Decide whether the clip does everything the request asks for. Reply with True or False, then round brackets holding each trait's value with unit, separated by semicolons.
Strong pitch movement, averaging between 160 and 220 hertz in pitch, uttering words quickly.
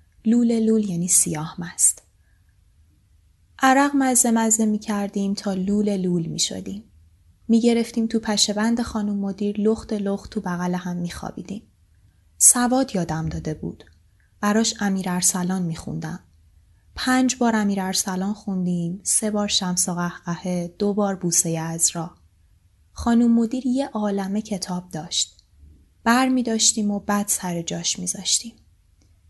False (5.9 semitones; 185 Hz; 135 wpm)